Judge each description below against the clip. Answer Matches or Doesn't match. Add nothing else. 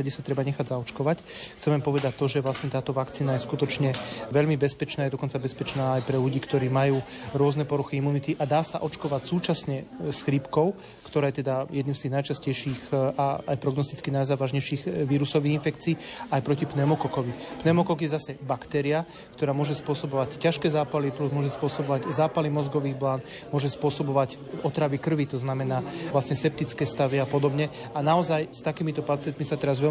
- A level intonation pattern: Matches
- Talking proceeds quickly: Matches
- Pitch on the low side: Doesn't match